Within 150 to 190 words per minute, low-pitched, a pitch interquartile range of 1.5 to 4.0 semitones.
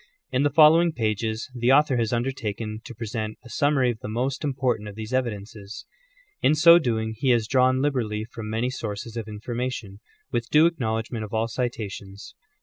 Yes: average, 175 wpm; low, 115 Hz; average, 3.1 semitones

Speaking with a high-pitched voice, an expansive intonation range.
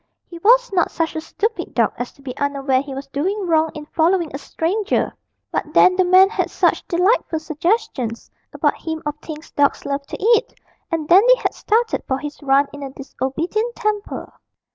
Yes: very high, 325 Hz; wide, 6.0 semitones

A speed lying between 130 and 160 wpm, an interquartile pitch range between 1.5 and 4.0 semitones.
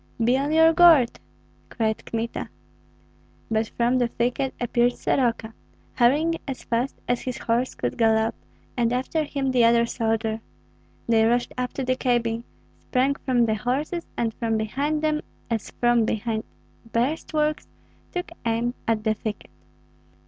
Yes: average, 150 wpm; average, 3.0 semitones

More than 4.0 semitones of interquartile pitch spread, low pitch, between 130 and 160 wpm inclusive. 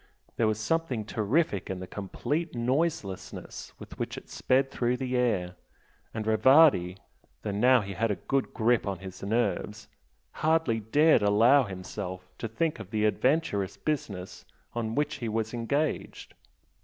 Yes: average, 4.9 semitones; low, 115 Hz; average, 150 wpm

